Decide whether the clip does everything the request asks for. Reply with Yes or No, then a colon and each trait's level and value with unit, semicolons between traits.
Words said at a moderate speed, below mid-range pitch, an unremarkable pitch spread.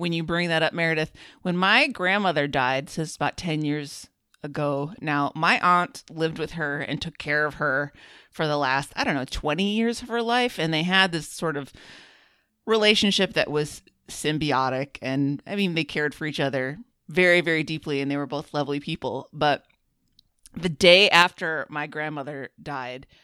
No: average, 185 wpm; medium, 155 Hz; average, 3.5 semitones